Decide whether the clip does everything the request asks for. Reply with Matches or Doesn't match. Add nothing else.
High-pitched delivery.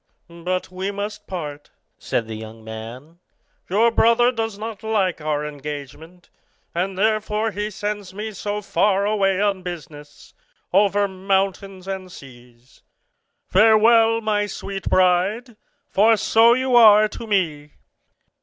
Matches